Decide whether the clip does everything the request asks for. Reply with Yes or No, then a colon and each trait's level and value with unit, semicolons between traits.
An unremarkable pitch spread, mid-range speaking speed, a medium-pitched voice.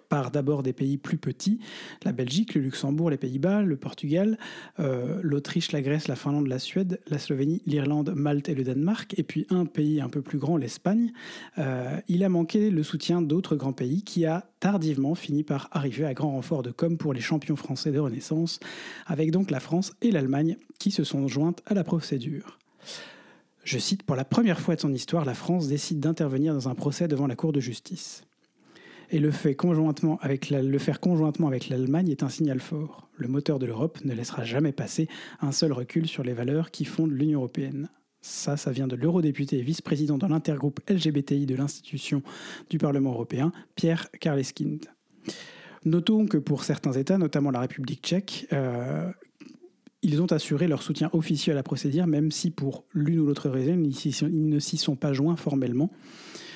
Yes: average, 3.1 semitones; average, 190 wpm; medium, 155 Hz